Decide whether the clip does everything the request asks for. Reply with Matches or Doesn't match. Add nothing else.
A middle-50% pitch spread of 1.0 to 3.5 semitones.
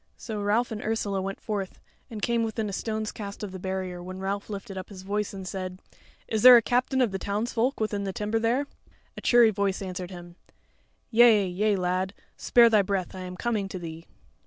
Matches